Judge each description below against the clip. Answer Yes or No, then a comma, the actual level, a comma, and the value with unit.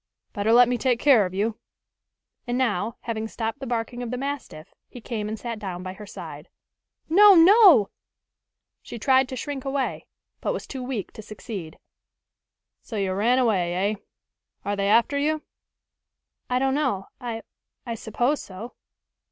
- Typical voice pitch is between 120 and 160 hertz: No, high, 235 Hz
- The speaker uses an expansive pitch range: No, average, 4.1 semitones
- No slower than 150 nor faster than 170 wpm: Yes, average, 165 wpm